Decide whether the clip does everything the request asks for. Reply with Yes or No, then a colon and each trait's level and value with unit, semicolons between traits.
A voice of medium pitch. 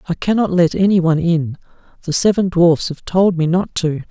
Yes: medium, 175 Hz